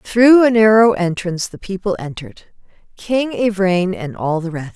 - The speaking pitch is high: Yes, high, 195 Hz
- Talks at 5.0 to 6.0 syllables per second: No, 4.8 syllables/s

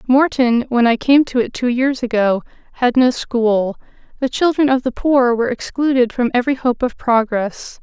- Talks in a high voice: Yes, very high, 250 Hz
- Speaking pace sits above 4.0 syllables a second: Yes, 4.8 syllables/s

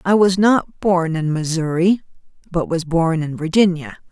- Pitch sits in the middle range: Yes, medium, 175 Hz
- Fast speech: No, average, 160 wpm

